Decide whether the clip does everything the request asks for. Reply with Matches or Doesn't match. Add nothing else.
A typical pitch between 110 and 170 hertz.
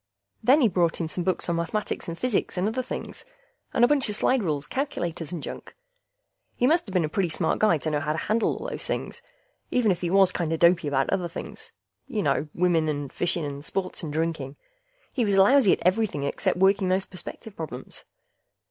Doesn't match